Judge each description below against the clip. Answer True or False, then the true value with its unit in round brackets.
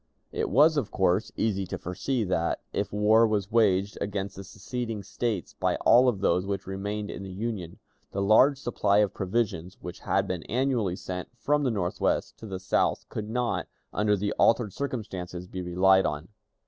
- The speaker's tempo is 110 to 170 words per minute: False (180 wpm)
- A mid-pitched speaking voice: False (100 Hz)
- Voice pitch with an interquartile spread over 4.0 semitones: False (3.4 semitones)